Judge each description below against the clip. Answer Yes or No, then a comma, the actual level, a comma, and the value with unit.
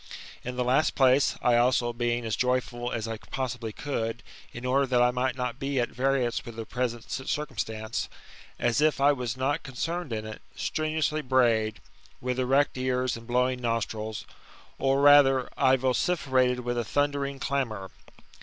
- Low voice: Yes, low, 125 Hz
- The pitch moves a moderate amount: No, narrow, 2.3 semitones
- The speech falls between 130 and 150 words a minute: No, average, 165 wpm